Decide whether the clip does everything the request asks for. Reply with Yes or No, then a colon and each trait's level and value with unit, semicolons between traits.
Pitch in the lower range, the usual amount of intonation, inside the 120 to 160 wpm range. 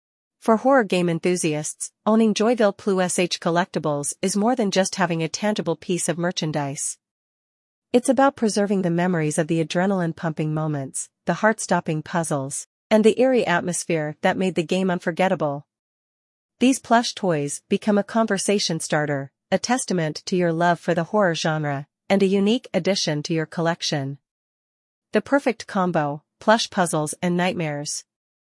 No: medium, 175 Hz; average, 4.5 semitones; average, 150 wpm